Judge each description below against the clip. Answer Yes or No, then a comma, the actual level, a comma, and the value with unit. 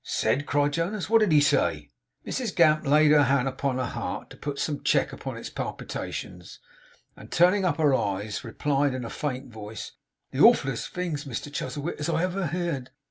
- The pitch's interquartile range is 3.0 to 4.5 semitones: Yes, average, 4.2 semitones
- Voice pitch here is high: No, medium, 145 Hz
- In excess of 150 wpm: Yes, average, 190 wpm